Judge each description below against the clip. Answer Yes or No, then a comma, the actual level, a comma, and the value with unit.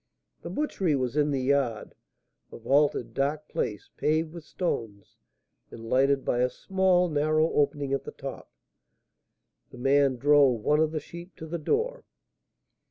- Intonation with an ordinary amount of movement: Yes, average, 3.2 semitones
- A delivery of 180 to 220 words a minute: No, average, 155 wpm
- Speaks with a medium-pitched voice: Yes, medium, 145 Hz